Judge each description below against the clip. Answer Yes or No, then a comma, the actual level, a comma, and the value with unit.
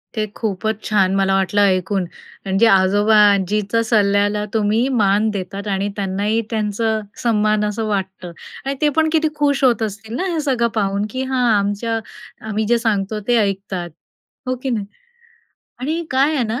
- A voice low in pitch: No, high, 210 Hz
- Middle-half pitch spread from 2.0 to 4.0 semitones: Yes, narrow, 2.6 semitones